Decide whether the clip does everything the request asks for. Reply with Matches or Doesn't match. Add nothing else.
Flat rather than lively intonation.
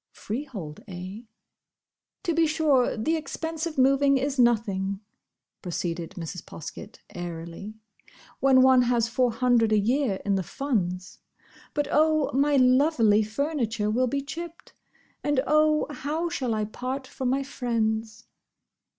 Doesn't match